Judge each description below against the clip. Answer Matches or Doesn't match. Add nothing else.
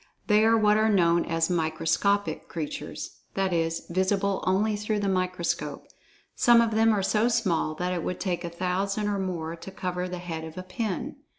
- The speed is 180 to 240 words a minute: Matches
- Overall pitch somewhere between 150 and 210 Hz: Matches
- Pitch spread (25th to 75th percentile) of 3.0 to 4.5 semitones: Matches